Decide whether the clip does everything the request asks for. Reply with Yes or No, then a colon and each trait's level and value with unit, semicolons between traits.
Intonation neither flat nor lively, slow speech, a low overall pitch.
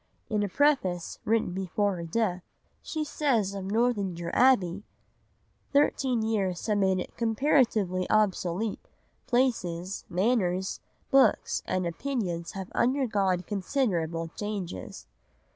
No: average, 4.6 semitones; slow, 105 wpm; high, 200 Hz